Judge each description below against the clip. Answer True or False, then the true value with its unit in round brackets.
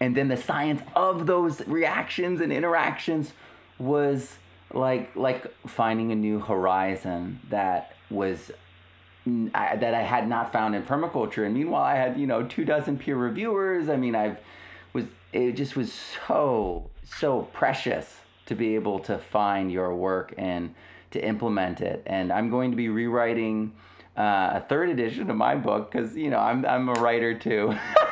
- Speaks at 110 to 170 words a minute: True (165 wpm)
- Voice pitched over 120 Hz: False (115 Hz)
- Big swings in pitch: True (6.6 semitones)